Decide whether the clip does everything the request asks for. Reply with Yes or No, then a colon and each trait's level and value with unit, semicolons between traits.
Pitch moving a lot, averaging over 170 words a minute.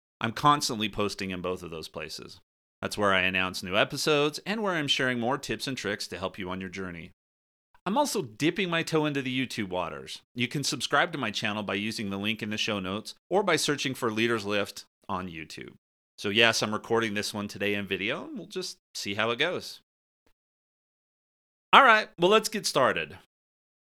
Yes: wide, 7.0 semitones; average, 200 wpm